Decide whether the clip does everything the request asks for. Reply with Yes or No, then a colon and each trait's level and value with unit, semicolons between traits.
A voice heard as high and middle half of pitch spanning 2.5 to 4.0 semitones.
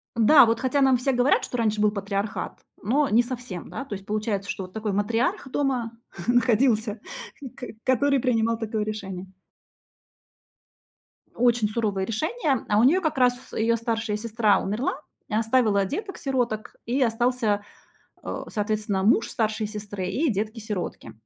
Yes: high, 225 Hz; average, 3.1 semitones